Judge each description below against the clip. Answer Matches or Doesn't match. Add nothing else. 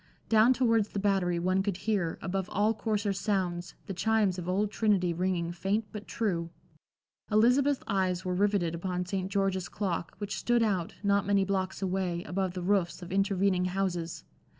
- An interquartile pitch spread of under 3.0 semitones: Matches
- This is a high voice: Matches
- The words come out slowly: Doesn't match